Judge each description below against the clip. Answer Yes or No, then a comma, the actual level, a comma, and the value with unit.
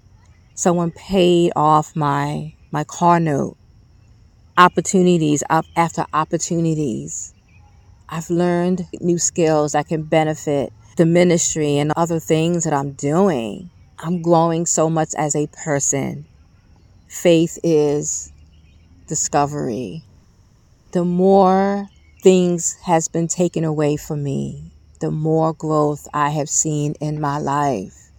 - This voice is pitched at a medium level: Yes, medium, 155 Hz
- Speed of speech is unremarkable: No, slow, 115 wpm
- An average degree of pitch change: No, wide, 7.3 semitones